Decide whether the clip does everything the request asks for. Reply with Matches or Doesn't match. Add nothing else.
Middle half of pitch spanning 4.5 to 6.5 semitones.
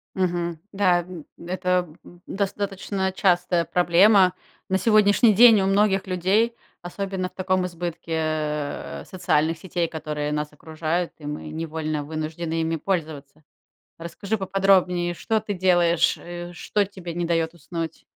Doesn't match